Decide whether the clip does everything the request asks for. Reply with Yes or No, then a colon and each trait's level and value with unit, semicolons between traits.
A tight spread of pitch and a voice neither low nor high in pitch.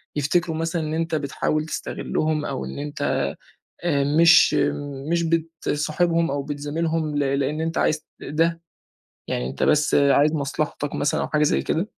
Yes: narrow, 2.2 semitones; medium, 155 Hz